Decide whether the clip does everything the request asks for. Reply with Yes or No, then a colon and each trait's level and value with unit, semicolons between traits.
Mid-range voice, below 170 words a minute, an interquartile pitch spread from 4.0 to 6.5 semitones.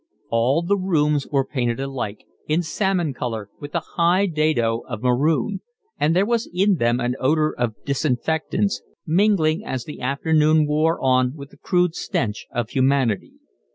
Yes: medium, 150 Hz; average, 155 wpm; average, 5.1 semitones